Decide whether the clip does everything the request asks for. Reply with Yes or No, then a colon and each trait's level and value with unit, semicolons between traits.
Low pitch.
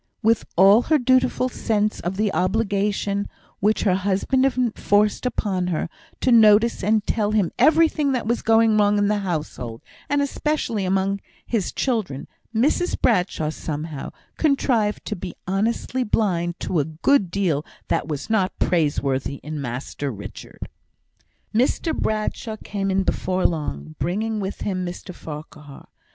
No: high, 200 Hz